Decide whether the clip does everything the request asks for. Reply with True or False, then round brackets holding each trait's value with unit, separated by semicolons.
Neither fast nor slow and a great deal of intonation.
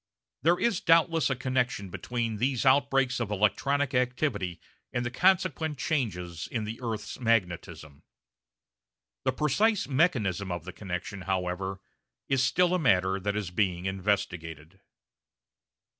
False (130 wpm; 6.5 semitones)